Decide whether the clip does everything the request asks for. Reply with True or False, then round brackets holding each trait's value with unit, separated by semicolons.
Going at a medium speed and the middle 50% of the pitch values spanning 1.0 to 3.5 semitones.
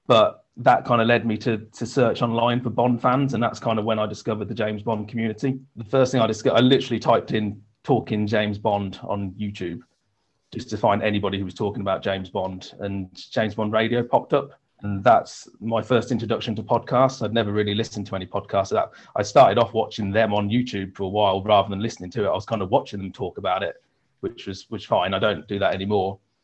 False (230 wpm; 2.7 semitones)